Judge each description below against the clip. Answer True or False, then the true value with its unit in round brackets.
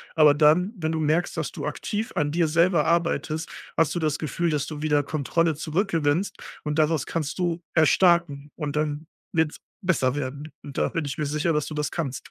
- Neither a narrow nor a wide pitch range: False (2.2 semitones)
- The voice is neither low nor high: True (155 Hz)